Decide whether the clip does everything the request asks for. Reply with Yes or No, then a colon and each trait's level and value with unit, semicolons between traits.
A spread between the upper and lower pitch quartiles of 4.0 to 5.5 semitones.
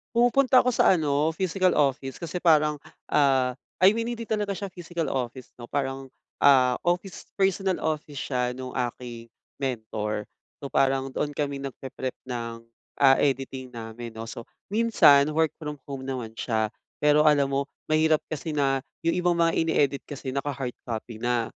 Yes: average, 4.3 semitones